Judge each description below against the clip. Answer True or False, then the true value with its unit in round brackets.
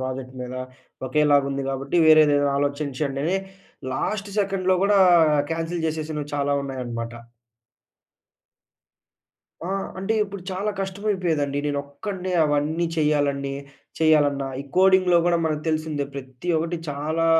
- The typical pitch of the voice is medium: True (150 Hz)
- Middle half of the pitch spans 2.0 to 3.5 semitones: False (4.0 semitones)